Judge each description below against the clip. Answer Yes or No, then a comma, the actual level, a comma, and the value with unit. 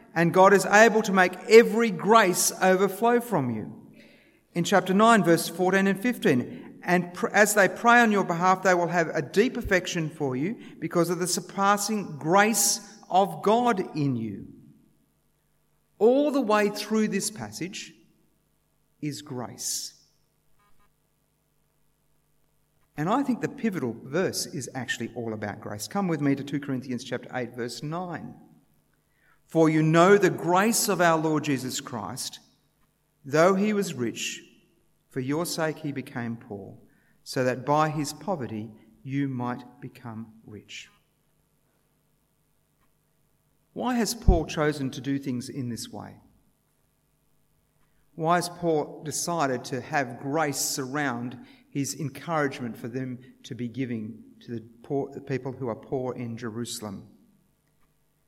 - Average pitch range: No, wide, 6.9 semitones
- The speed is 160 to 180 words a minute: No, average, 140 wpm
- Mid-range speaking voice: Yes, medium, 155 Hz